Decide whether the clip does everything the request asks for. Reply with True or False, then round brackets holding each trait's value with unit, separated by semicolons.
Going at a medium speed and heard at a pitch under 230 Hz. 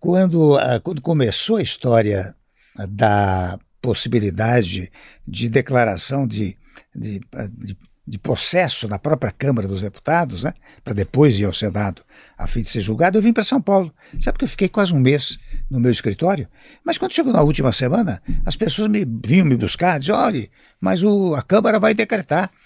True (175 wpm; 135 Hz)